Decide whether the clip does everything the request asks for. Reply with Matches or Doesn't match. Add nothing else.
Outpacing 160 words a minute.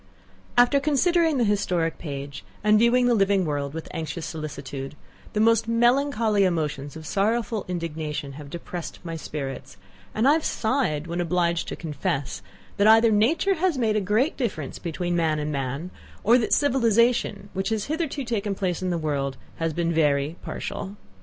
Matches